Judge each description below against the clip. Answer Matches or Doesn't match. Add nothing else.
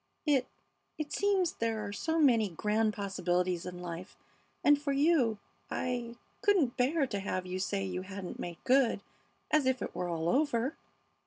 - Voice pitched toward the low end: Doesn't match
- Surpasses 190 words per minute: Doesn't match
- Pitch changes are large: Matches